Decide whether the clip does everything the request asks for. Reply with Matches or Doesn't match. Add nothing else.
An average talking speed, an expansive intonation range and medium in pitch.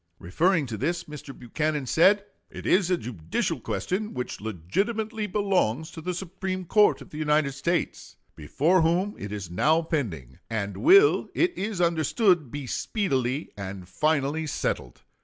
Matches